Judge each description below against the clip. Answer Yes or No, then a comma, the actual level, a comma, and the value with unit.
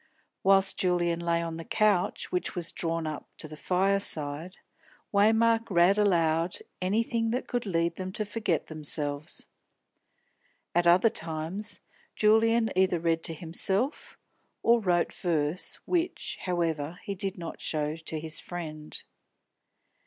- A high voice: No, medium, 175 Hz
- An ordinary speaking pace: No, slow, 130 wpm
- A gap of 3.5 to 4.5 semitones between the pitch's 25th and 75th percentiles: Yes, average, 3.9 semitones